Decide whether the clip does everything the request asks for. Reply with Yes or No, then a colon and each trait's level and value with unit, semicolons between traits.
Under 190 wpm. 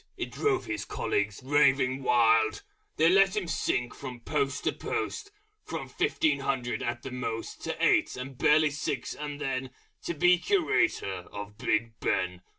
Yes: average, 155 wpm